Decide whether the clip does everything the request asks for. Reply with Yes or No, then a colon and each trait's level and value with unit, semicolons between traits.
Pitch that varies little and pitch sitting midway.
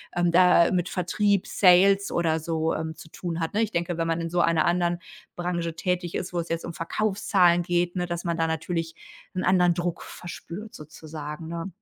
Yes: narrow, 1.5 semitones; medium, 175 Hz